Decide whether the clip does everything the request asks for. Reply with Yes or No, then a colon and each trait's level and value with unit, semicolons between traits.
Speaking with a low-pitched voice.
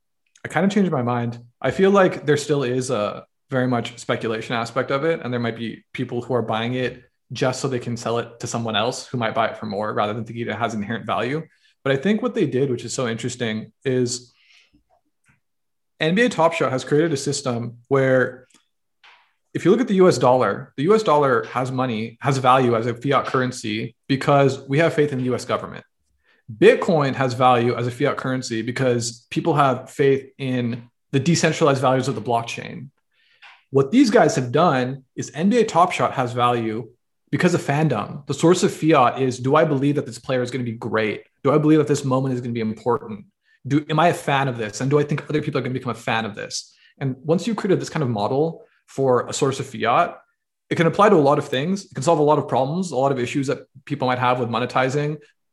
Yes: low, 130 Hz